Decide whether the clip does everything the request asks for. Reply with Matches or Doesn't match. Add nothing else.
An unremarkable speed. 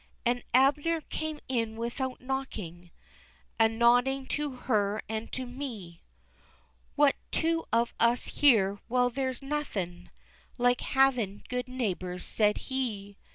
Doesn't match